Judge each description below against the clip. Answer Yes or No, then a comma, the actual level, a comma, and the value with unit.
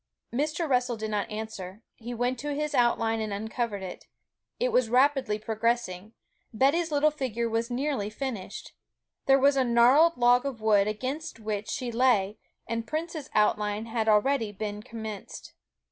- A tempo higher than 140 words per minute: Yes, average, 155 wpm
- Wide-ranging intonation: No, average, 4.0 semitones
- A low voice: No, high, 235 Hz